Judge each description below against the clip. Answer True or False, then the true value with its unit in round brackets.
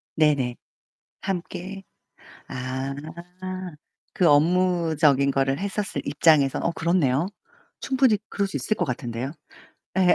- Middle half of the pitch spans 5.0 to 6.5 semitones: True (5.3 semitones)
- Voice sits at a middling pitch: True (160 Hz)